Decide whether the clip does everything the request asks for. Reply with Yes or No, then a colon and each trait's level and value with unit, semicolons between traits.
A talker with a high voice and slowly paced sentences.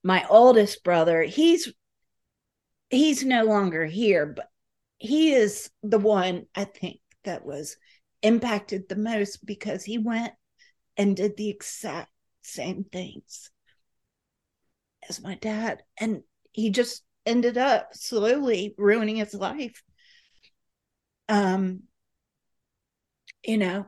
Yes: high, 215 Hz; slow, 110 wpm